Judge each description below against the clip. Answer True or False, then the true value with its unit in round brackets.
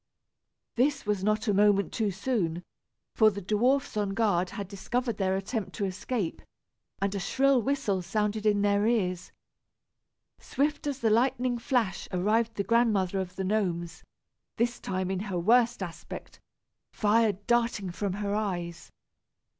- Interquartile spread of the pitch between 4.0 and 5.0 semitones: False (3.4 semitones)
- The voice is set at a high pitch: True (205 Hz)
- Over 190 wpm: False (145 wpm)